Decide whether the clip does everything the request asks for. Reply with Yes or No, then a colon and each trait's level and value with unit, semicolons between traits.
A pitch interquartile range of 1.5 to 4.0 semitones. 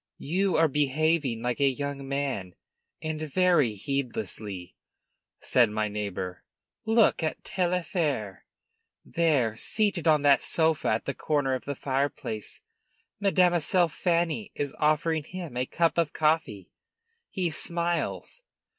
No: average, 5.0 semitones